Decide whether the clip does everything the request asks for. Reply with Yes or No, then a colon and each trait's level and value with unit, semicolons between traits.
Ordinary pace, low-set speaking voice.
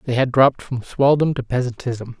Yes: average, 190 wpm; low, 125 Hz